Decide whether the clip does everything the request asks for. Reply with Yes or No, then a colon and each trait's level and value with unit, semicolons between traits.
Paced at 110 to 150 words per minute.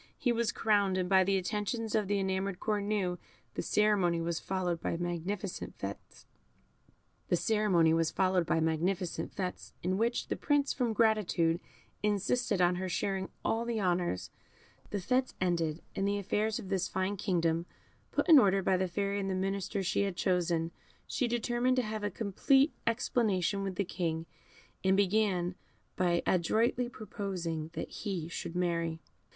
Yes: average, 145 wpm